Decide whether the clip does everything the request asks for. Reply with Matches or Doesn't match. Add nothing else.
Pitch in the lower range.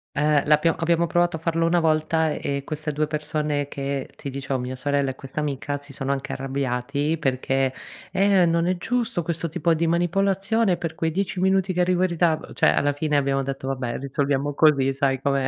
Doesn't match